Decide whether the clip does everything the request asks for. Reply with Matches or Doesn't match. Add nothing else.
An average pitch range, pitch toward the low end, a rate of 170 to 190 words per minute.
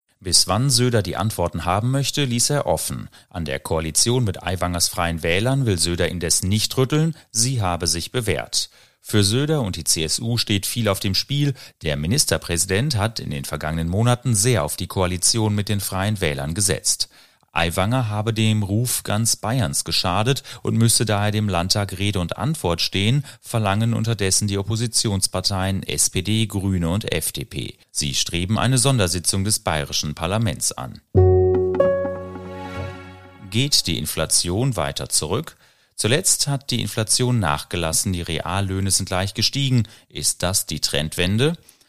Doesn't match